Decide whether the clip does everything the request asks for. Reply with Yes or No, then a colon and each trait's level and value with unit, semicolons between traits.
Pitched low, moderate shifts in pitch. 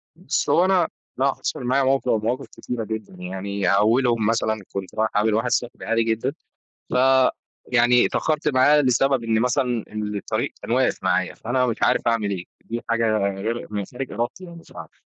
Yes: low, 115 Hz; average, 3.2 semitones